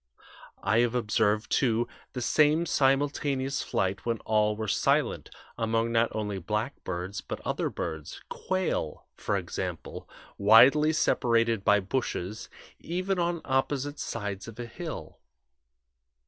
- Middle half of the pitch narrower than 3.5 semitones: No, average, 4.9 semitones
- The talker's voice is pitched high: No, low, 115 Hz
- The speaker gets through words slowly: Yes, slow, 120 wpm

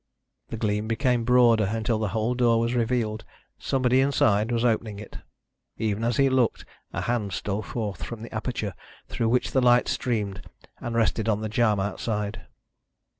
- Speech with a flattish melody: Yes, narrow, 2.2 semitones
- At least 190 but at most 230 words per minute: No, average, 170 wpm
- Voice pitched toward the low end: Yes, low, 115 Hz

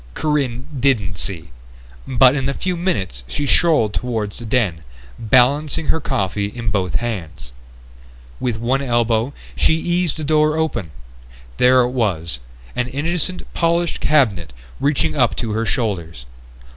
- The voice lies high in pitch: No, low, 125 Hz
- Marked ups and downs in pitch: Yes, wide, 6.3 semitones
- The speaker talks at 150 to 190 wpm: No, average, 140 wpm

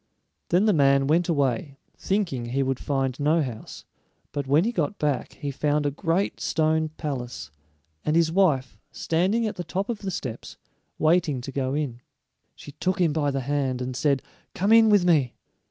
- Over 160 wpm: Yes, average, 185 wpm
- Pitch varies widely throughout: No, average, 4.6 semitones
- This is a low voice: No, medium, 150 Hz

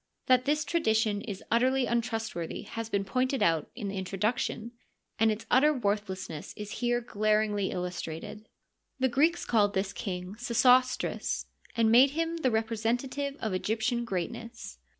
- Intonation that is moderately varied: Yes, average, 3.8 semitones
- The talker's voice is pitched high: Yes, high, 225 Hz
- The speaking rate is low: No, average, 145 wpm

